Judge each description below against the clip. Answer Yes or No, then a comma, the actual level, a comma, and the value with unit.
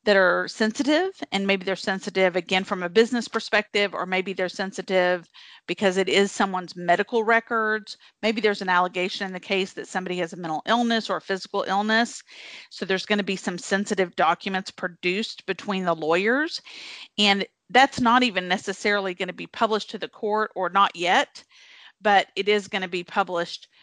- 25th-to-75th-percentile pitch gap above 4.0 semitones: No, average, 2.7 semitones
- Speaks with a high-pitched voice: Yes, high, 195 Hz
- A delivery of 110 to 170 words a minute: No, average, 185 wpm